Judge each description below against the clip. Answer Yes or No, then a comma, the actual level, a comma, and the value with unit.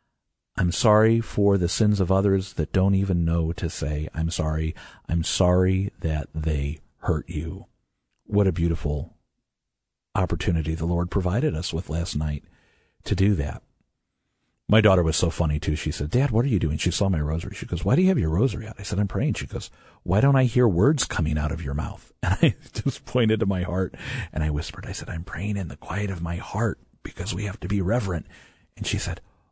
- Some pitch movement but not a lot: Yes, average, 4.2 semitones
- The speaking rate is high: Yes, fast, 215 wpm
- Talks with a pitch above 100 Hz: No, very low, 90 Hz